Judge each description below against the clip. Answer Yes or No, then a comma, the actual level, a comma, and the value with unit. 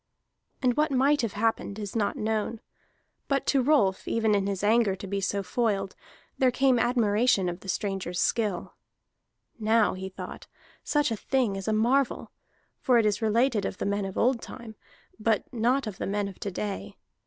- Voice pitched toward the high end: Yes, high, 220 Hz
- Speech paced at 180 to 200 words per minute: Yes, average, 185 wpm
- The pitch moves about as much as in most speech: Yes, average, 3.5 semitones